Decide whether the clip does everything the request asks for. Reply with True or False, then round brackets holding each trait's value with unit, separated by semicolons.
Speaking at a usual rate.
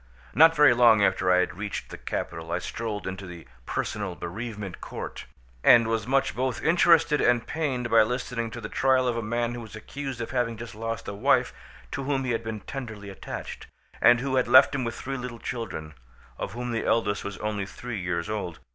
False (210 wpm)